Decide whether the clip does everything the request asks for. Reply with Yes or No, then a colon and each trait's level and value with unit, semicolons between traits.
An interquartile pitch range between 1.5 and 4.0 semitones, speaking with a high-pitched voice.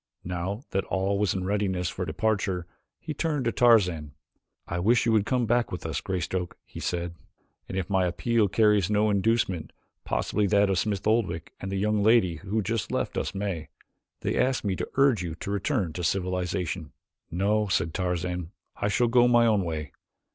No: average, 3.5 semitones; low, 100 Hz